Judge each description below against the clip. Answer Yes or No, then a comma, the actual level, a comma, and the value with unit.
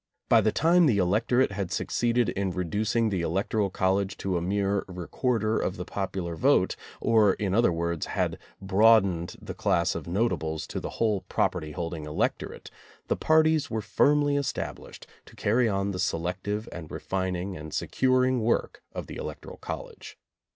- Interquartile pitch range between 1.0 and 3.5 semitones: No, average, 4.1 semitones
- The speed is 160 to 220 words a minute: Yes, average, 165 wpm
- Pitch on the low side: Yes, low, 100 Hz